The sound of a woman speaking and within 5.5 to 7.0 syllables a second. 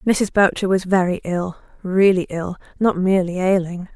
No: female; 4.8 syllables/s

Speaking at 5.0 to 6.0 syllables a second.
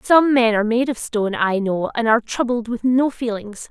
Yes: 5.3 syllables/s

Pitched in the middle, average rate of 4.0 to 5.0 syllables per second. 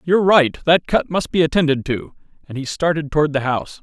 No: medium, 155 Hz; 6.0 syllables/s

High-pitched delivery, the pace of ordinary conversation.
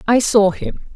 Yes: high, 220 Hz; average, 190 wpm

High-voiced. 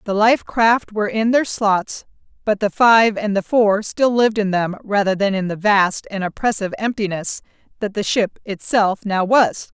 Yes: high, 210 Hz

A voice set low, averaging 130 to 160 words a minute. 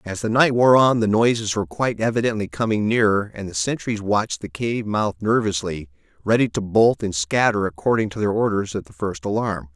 No: low, 110 Hz; fast, 205 wpm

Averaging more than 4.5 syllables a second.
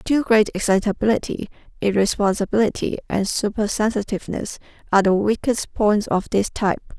Yes: 5.4 syllables/s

